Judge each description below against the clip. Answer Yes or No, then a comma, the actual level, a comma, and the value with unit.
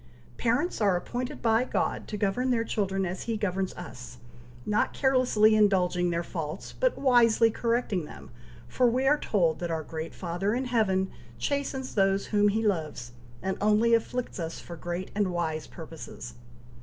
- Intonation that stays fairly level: No, average, 5.0 semitones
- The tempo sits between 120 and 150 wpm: No, average, 165 wpm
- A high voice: Yes, high, 205 Hz